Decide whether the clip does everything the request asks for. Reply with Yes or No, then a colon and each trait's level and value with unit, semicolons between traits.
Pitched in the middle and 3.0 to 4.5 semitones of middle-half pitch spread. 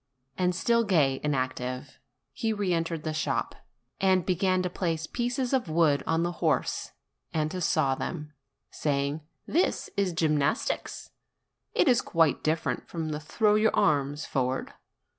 Yes: medium, 165 Hz; average, 4.1 semitones